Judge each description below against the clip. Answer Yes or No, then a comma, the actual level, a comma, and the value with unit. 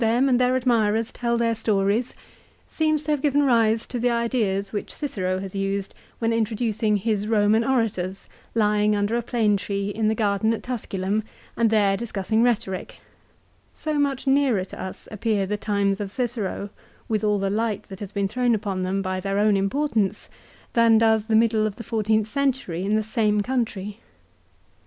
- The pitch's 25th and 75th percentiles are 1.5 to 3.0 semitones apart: Yes, average, 2.7 semitones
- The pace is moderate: Yes, average, 180 wpm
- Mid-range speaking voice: No, high, 215 Hz